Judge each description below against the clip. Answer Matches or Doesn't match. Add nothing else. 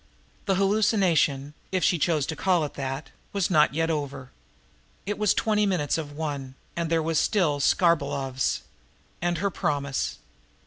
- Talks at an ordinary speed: Matches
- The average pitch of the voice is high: Doesn't match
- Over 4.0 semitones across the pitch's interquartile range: Matches